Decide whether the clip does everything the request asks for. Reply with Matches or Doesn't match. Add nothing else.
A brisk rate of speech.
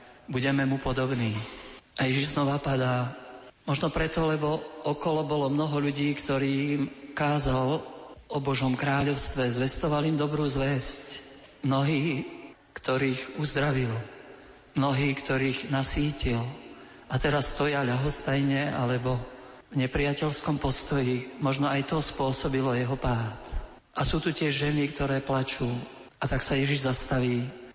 Doesn't match